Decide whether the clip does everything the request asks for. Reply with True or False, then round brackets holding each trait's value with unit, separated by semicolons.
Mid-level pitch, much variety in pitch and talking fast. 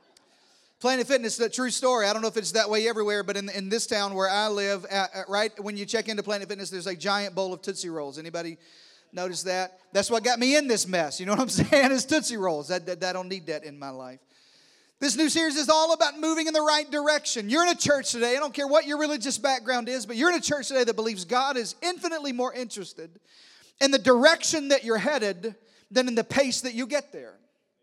False (230 Hz; 5.9 semitones; 250 wpm)